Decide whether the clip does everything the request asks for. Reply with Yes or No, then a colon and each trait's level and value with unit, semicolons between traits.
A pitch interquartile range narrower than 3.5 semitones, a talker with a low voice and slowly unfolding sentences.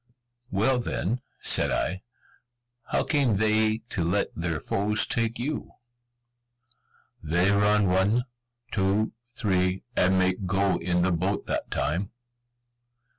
Yes: average, 2.9 semitones; low, 100 Hz; slow, 120 wpm